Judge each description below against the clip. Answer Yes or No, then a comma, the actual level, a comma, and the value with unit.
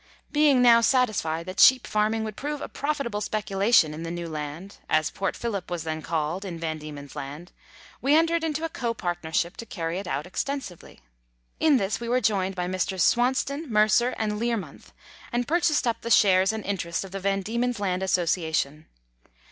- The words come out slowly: No, average, 185 wpm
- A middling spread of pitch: No, wide, 5.8 semitones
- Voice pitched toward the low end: No, high, 200 Hz